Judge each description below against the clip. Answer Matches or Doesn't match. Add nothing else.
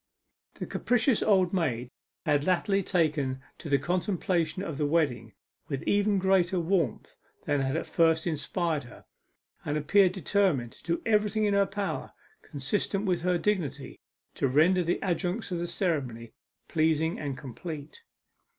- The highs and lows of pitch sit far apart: Doesn't match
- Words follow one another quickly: Doesn't match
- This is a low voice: Doesn't match